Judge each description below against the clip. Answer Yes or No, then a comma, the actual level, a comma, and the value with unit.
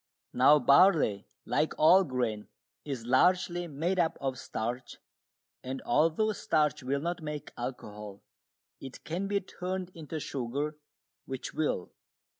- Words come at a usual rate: No, slow, 125 wpm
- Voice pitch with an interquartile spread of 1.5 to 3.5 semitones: No, average, 5.3 semitones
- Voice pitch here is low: No, medium, 150 Hz